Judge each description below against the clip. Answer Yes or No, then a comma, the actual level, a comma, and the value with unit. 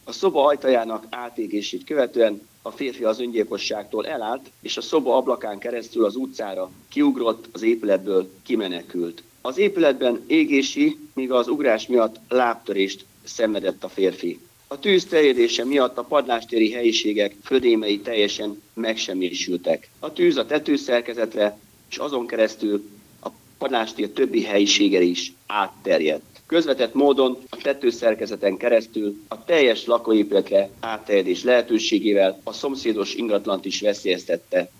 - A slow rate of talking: No, average, 120 wpm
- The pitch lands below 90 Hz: No, low, 115 Hz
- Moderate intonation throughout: No, wide, 7.9 semitones